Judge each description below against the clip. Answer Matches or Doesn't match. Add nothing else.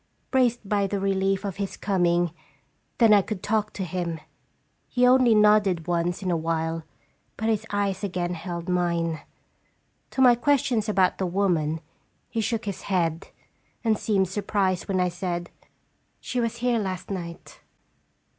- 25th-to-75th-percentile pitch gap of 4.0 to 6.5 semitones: Doesn't match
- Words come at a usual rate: Matches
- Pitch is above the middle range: Matches